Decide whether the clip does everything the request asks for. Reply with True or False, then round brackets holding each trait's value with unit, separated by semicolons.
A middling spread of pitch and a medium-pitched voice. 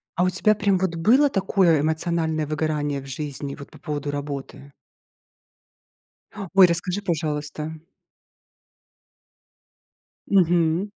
True (3.8 semitones; 160 Hz)